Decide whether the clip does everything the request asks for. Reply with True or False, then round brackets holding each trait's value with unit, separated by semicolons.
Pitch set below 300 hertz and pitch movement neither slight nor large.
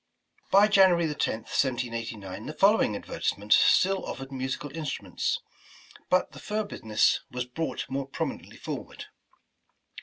False (135 Hz; 7.3 semitones)